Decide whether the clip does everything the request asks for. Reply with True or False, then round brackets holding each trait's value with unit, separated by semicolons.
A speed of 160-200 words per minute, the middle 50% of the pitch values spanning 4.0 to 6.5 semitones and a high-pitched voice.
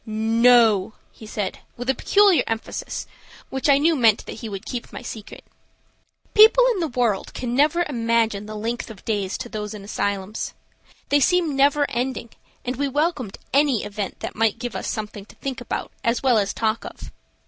True (185 wpm; 4.4 semitones; 235 Hz)